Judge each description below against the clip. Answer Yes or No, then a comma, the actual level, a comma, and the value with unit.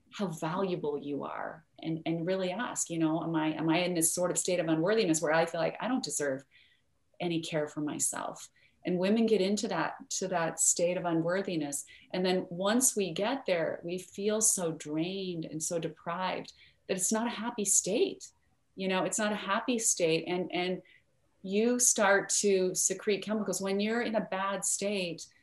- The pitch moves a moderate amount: Yes, average, 3.6 semitones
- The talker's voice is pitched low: No, medium, 185 Hz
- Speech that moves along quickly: No, average, 190 wpm